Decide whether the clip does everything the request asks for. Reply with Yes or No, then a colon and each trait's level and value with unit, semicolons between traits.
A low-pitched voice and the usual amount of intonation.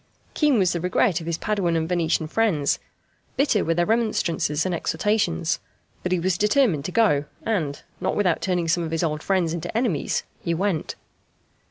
No: medium, 175 Hz; average, 4.3 semitones